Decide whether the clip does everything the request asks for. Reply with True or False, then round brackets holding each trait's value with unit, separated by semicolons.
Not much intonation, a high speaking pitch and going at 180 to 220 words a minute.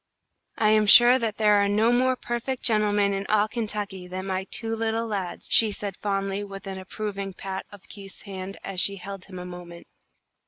True (2.0 semitones; 200 Hz; 195 wpm)